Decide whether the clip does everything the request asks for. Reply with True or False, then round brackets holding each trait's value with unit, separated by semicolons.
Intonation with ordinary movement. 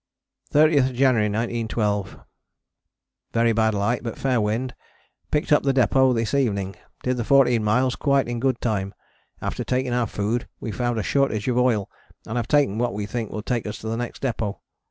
True (3.1 semitones)